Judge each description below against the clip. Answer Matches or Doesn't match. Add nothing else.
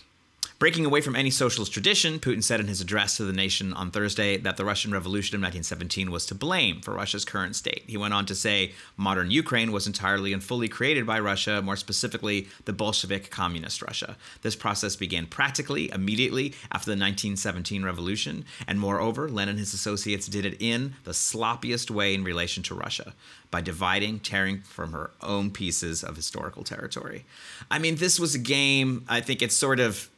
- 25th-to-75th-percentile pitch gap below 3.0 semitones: Doesn't match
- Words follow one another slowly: Doesn't match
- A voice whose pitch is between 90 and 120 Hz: Matches